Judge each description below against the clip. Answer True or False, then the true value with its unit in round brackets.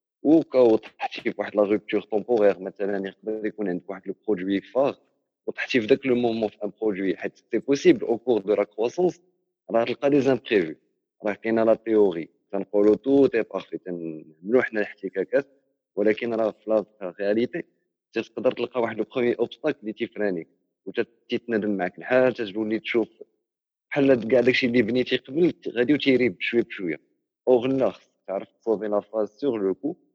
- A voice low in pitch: True (115 Hz)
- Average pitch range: True (3.9 semitones)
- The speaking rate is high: True (160 wpm)